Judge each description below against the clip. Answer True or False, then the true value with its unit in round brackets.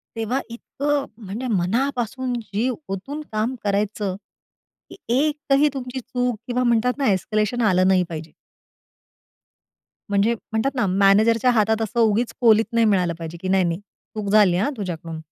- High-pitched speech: True (220 Hz)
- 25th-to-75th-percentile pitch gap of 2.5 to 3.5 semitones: False (4.1 semitones)